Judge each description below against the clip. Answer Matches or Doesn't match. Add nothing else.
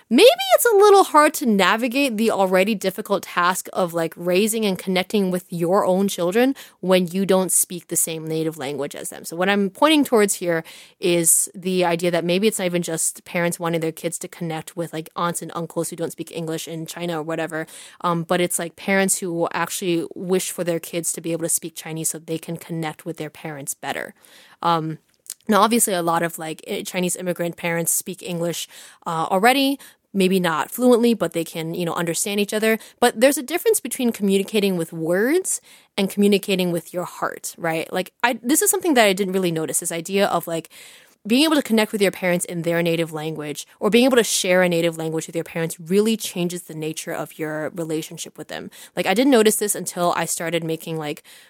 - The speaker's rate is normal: Doesn't match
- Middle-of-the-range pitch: Matches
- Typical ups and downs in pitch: Matches